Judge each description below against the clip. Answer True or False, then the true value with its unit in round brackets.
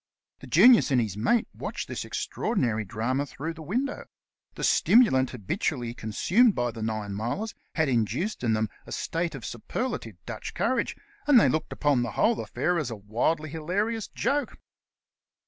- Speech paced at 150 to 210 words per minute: True (165 wpm)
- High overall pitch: False (145 Hz)